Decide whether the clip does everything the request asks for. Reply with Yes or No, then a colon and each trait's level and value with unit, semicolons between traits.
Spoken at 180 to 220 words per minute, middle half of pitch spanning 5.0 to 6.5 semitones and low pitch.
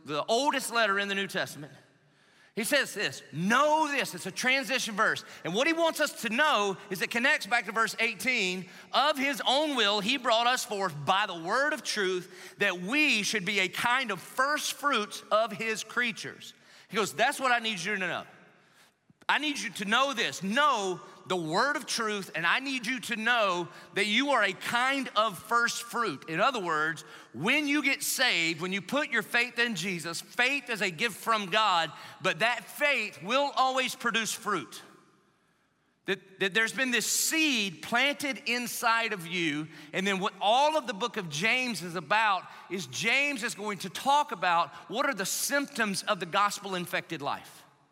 No: average, 190 wpm; wide, 5.5 semitones; high, 225 Hz